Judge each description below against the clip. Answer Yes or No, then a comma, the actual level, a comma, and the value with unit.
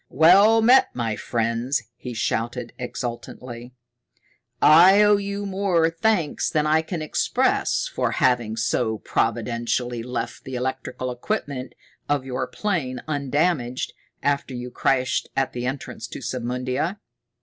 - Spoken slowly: Yes, slow, 125 wpm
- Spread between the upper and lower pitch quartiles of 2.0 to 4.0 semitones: No, average, 5.1 semitones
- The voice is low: Yes, low, 130 Hz